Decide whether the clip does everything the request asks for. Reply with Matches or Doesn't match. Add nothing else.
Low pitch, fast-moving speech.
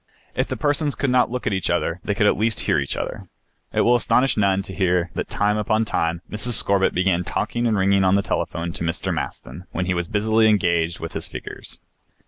Matches